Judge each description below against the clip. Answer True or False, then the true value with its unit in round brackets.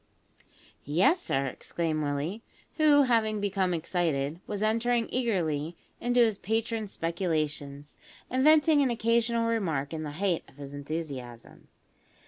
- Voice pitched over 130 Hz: True (190 Hz)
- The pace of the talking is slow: True (125 wpm)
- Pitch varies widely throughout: True (7.2 semitones)